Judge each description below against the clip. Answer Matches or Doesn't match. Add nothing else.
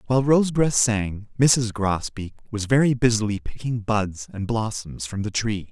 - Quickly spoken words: Doesn't match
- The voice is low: Matches